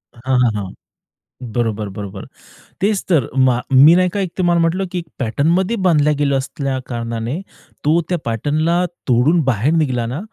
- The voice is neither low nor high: Yes, medium, 145 Hz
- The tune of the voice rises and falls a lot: Yes, wide, 6.2 semitones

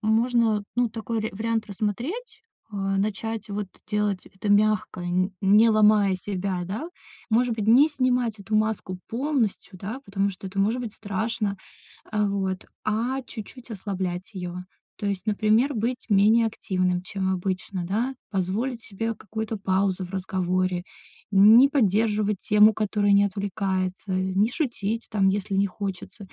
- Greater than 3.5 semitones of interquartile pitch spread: No, average, 2.8 semitones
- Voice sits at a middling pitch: No, high, 210 Hz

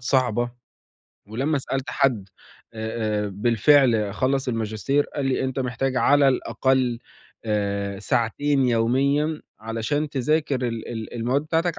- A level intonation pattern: No, average, 3.7 semitones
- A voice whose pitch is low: Yes, low, 125 Hz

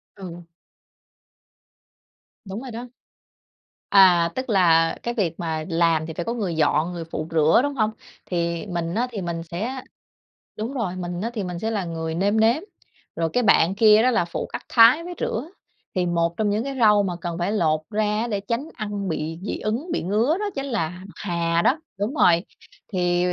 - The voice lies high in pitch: Yes, high, 195 Hz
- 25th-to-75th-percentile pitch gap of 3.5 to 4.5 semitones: No, average, 5.0 semitones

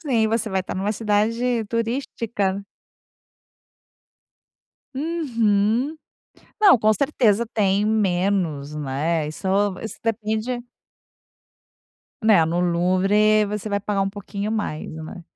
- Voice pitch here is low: No, high, 210 Hz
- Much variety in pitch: No, average, 3.2 semitones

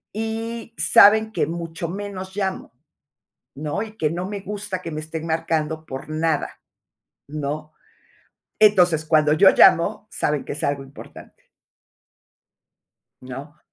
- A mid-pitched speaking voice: Yes, medium, 165 Hz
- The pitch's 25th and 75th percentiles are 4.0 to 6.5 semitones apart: Yes, average, 4.9 semitones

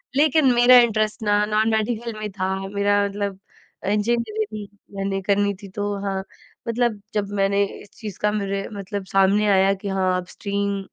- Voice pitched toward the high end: Yes, high, 205 Hz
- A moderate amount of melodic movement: No, narrow, 1.6 semitones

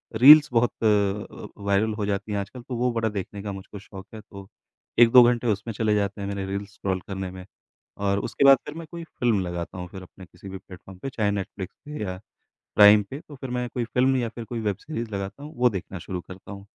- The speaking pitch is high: No, low, 105 Hz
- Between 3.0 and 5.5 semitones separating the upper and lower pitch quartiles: Yes, average, 3.6 semitones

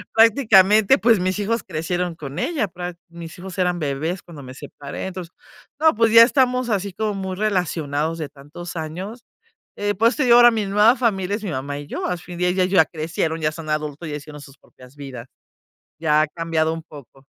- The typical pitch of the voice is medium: Yes, medium, 175 Hz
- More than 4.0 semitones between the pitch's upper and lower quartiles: Yes, average, 5.2 semitones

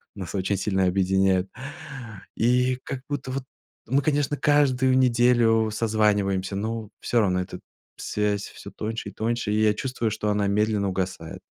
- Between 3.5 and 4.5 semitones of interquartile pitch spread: Yes, average, 3.9 semitones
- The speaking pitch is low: Yes, low, 110 Hz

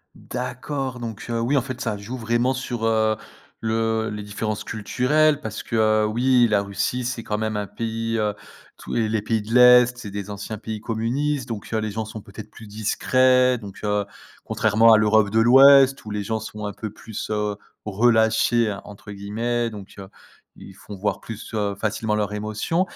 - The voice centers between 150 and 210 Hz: No, low, 110 Hz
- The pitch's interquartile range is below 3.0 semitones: Yes, narrow, 2.4 semitones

